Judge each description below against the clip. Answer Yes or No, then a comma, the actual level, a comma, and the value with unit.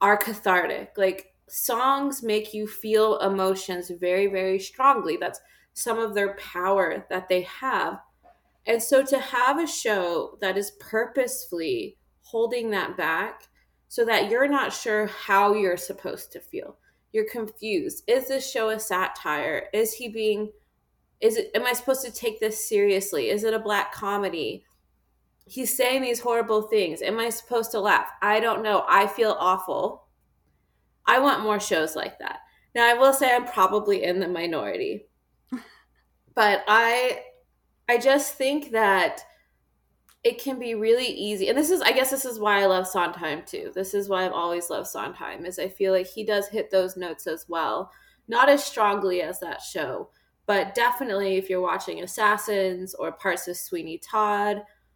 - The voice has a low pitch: No, high, 215 Hz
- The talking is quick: No, average, 170 wpm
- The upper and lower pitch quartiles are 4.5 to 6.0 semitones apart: Yes, average, 4.9 semitones